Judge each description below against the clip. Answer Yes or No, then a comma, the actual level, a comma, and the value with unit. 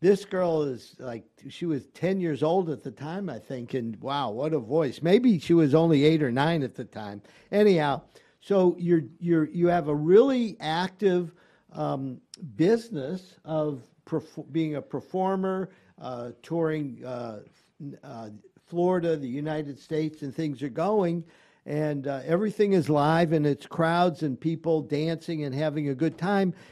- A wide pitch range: No, average, 3.6 semitones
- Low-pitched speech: No, medium, 160 Hz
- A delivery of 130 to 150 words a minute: No, average, 165 wpm